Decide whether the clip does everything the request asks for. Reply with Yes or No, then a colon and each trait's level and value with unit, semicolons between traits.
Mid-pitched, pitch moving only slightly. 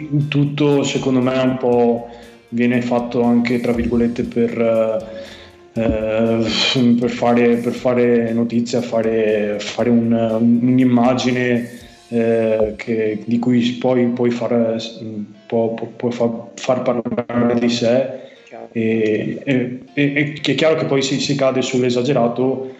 No: low, 120 Hz; narrow, 1.7 semitones